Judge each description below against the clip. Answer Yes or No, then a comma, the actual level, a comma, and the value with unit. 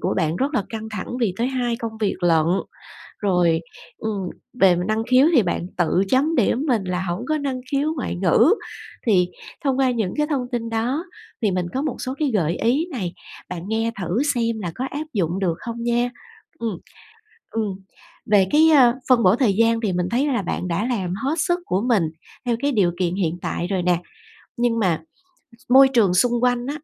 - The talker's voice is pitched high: Yes, high, 225 Hz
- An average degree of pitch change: No, wide, 5.7 semitones